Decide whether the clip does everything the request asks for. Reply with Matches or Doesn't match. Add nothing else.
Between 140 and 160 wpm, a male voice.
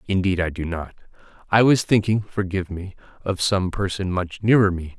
Matches